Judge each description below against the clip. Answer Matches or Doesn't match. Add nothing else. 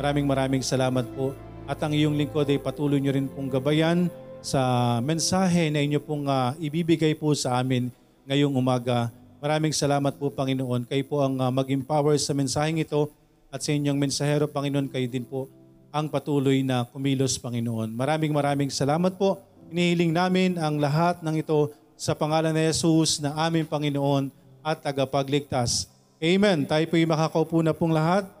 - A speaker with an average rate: Doesn't match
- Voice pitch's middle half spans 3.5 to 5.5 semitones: Doesn't match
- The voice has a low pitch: Doesn't match